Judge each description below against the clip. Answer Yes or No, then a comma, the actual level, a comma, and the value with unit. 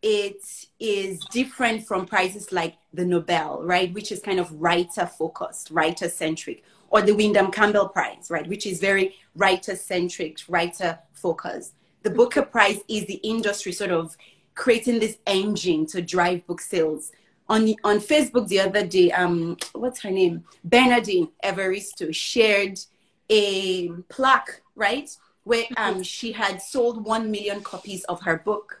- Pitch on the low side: No, high, 195 Hz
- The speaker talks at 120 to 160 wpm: Yes, average, 150 wpm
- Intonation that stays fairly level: No, average, 3.7 semitones